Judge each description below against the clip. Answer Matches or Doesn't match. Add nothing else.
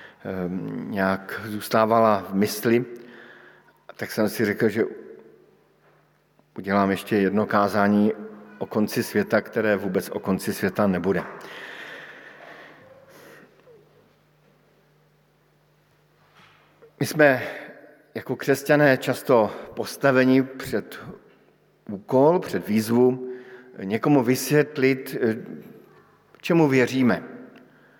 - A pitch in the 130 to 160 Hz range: Doesn't match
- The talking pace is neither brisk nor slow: Doesn't match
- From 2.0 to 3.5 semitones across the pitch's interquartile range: Doesn't match